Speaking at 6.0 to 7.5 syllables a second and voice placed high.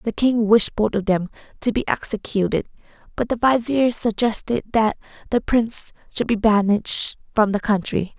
No: 5.1 syllables/s; high, 220 Hz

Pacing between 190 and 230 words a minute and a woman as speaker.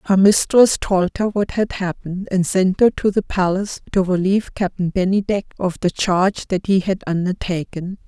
No: average, 180 wpm; female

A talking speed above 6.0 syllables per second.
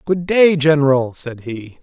No: 4.1 syllables/s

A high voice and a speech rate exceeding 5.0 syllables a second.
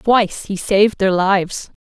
No: high, 200 Hz; 4.7 syllables/s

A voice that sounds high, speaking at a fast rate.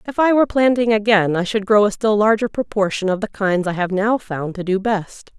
Yes: high, 210 Hz; fast, 245 wpm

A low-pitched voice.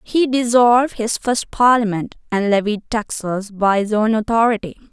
No: high, 220 Hz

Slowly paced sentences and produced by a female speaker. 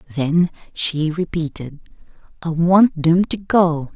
Yes: slow, 120 wpm; female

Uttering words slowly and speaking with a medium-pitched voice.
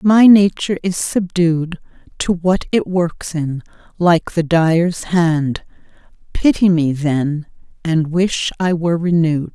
Yes: slow, 130 wpm; medium, 170 Hz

